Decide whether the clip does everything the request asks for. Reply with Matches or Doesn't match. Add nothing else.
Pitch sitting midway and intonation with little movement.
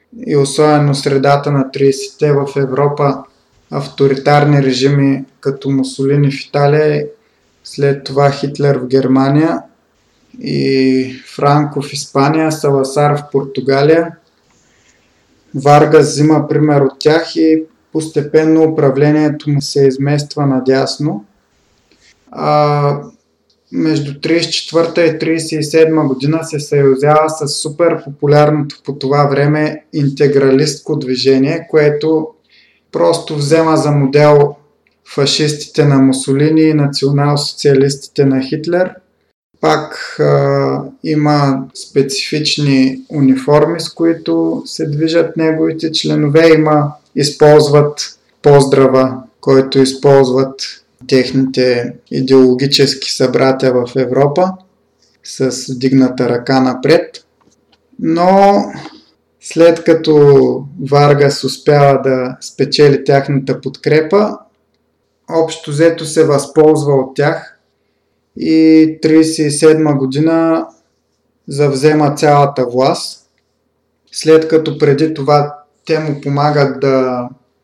Matches